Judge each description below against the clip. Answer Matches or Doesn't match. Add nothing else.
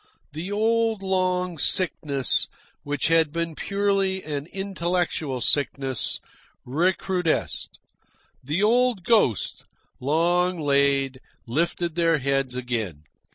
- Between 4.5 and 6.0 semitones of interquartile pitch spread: Matches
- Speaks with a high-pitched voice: Doesn't match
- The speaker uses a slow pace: Matches